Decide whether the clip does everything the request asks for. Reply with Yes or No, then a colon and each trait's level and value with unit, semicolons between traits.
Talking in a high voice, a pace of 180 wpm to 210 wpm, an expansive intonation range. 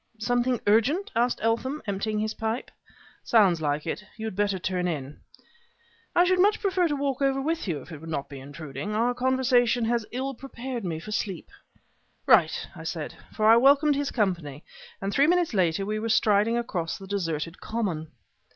Yes: high, 220 Hz; average, 185 wpm; wide, 6.5 semitones